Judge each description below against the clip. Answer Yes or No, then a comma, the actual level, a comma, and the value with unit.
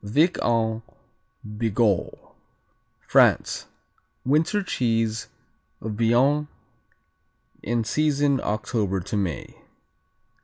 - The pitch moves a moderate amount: Yes, average, 4.8 semitones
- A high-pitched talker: No, low, 115 Hz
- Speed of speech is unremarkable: No, slow, 75 wpm